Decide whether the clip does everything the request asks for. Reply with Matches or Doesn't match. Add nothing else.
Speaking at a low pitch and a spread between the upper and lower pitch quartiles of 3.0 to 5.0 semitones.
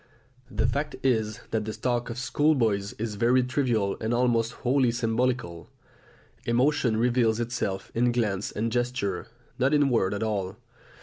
Doesn't match